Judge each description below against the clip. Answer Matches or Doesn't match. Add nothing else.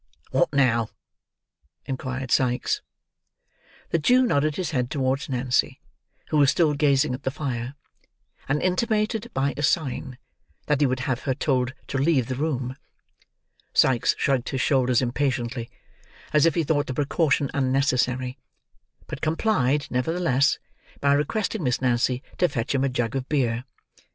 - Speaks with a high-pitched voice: Doesn't match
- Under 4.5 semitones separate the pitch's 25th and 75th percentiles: Matches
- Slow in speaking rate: Doesn't match